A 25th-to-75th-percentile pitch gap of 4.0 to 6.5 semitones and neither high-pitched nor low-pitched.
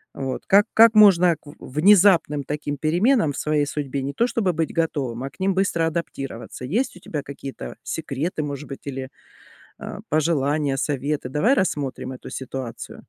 Yes: average, 4.5 semitones; medium, 150 Hz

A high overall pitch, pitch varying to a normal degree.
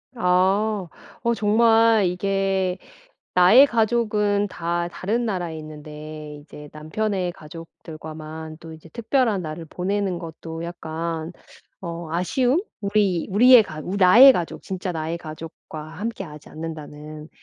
No: medium, 180 Hz; average, 4.6 semitones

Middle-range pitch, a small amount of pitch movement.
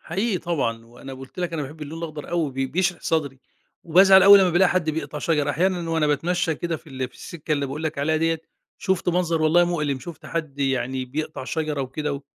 No: medium, 155 Hz; average, 3.5 semitones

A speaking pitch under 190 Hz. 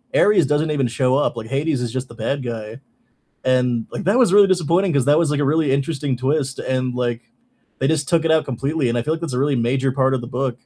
Yes: low, 135 Hz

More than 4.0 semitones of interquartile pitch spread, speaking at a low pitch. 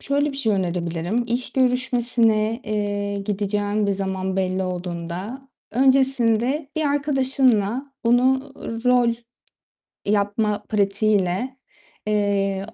No: average, 4.5 semitones; high, 215 Hz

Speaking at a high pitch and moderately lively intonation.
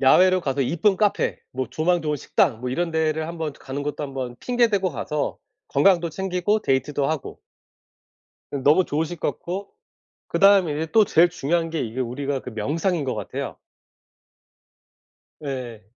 No: medium, 155 Hz; average, 4.9 semitones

